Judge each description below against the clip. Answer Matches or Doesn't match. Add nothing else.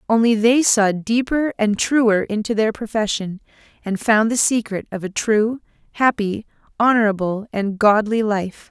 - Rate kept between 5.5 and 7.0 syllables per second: Doesn't match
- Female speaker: Matches